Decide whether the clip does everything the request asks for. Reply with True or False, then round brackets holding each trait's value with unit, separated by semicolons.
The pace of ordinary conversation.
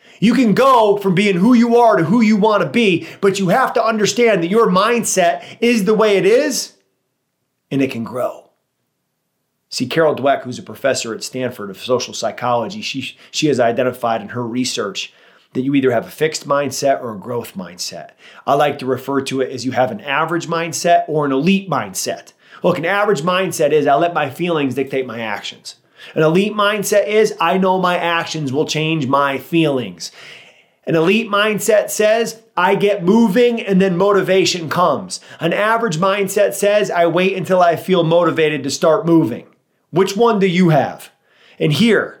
True (185 wpm)